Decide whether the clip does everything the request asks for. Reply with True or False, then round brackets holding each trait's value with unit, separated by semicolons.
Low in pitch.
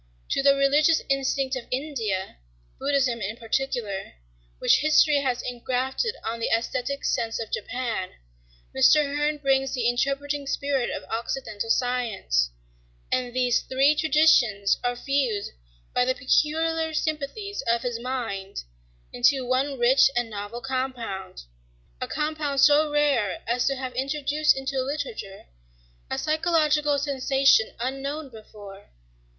False (260 Hz)